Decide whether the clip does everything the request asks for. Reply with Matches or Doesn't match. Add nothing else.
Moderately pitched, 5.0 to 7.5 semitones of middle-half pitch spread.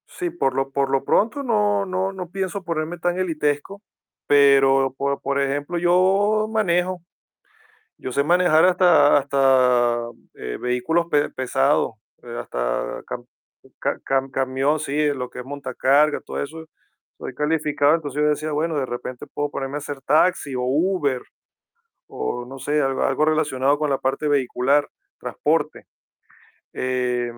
Doesn't match